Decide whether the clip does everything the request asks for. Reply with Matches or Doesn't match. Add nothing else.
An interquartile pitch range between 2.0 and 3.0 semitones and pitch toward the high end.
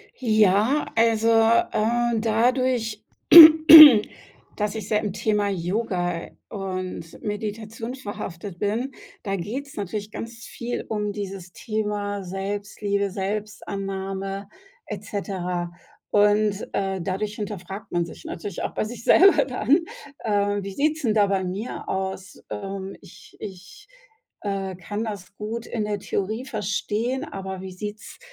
Matches